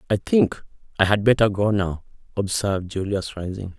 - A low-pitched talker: Yes, low, 100 Hz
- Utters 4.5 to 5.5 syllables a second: Yes, 5.1 syllables/s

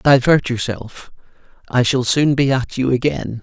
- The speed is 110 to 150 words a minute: Yes, average, 140 wpm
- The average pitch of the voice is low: Yes, low, 130 Hz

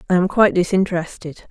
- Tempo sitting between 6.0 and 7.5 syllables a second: Yes, 6.9 syllables/s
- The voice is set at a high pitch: No, medium, 180 Hz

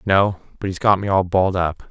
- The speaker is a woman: No, male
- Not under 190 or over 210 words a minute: No, fast, 220 wpm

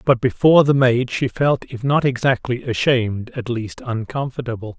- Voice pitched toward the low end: Yes, low, 125 Hz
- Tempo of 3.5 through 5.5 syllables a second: Yes, 4.9 syllables/s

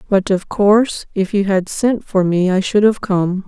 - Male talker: No, female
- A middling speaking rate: No, fast, 225 wpm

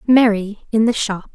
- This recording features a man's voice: No, female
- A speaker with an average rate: Yes, average, 180 wpm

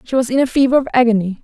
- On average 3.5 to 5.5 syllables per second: No, 7.5 syllables/s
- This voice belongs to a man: No, female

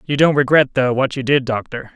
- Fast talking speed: Yes, fast, 245 wpm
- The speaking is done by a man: Yes, male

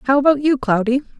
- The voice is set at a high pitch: Yes, very high, 265 Hz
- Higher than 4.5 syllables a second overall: Yes, 5.9 syllables/s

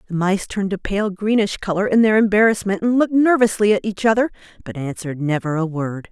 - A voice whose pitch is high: Yes, high, 200 Hz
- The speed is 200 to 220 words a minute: Yes, fast, 205 wpm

